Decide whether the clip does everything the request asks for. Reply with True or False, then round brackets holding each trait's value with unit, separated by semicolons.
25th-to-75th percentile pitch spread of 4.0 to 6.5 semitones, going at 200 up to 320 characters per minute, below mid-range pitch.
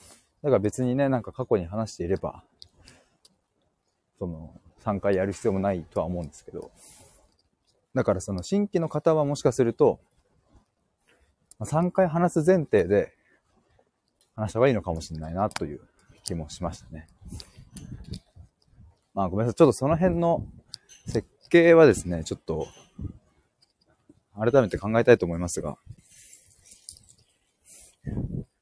False (7.1 semitones; 260 characters per minute; 105 Hz)